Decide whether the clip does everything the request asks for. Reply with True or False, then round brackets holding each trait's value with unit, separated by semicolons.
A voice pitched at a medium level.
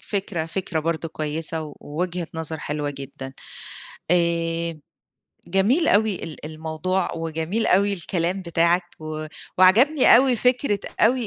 True (170 Hz)